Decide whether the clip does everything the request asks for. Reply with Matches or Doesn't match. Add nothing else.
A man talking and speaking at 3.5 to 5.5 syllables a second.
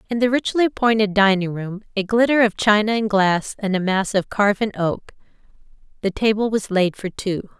Doesn't match